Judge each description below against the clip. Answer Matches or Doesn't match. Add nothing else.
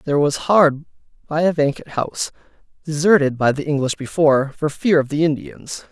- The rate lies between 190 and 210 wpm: Doesn't match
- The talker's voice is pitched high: Doesn't match